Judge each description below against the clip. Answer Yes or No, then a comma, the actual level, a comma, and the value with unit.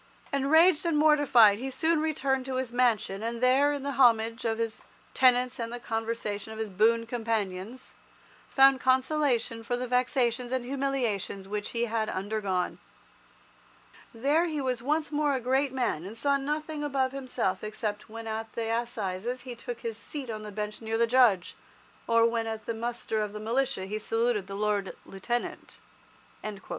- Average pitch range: Yes, average, 3.3 semitones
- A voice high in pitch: Yes, high, 235 Hz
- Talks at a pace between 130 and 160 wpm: No, average, 170 wpm